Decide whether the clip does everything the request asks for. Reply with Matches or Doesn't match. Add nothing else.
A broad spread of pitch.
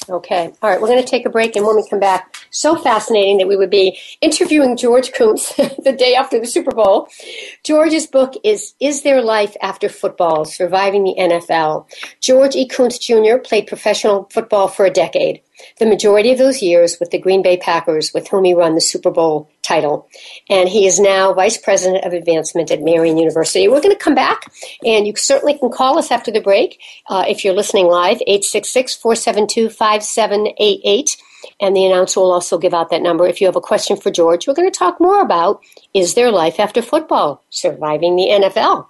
Matches